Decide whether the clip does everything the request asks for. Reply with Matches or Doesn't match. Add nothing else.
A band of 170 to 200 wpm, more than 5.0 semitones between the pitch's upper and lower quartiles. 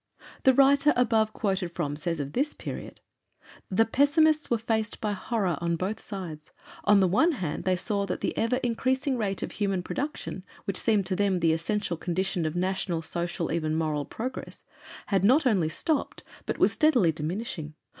Matches